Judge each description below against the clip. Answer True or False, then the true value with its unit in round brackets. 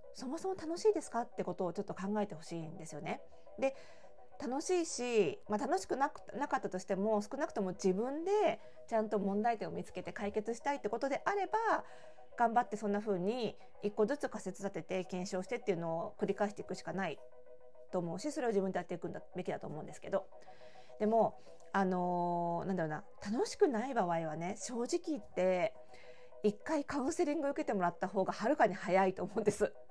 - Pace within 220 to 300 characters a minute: False (415 characters per minute)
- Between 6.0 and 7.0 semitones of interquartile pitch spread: True (6.5 semitones)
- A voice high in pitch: True (205 Hz)